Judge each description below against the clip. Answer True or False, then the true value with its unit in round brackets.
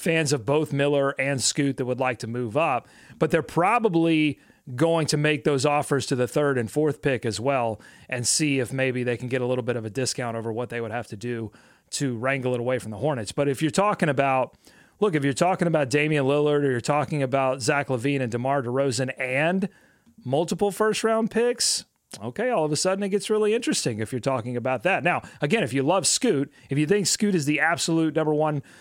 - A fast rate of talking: True (230 wpm)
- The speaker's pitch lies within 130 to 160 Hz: True (140 Hz)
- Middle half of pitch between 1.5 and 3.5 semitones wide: False (4.1 semitones)